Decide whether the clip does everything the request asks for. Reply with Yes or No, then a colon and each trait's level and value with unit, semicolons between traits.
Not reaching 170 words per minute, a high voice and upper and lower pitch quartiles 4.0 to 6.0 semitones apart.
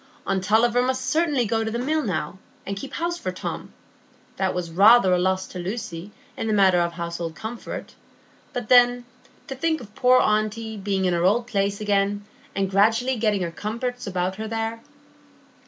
No: average, 180 wpm; high, 215 Hz; average, 4.3 semitones